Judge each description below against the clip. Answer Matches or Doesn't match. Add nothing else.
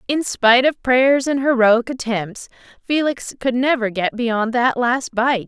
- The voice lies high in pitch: Matches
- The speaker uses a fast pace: Doesn't match